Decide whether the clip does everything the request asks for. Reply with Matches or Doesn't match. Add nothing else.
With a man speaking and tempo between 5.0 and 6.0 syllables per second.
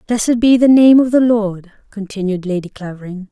Doesn't match